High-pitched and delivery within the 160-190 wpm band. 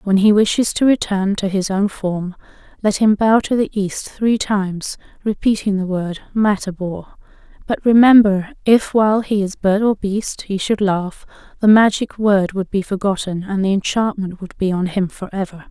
Yes: high, 200 Hz; average, 180 wpm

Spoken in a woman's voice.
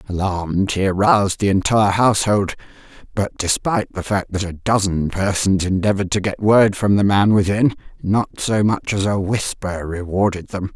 Yes: female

